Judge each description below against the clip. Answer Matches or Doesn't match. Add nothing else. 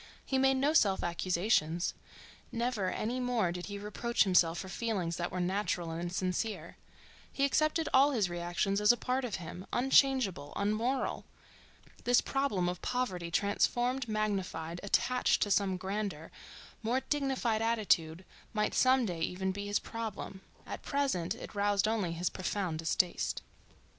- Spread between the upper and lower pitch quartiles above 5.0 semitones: Matches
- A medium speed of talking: Matches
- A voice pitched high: Matches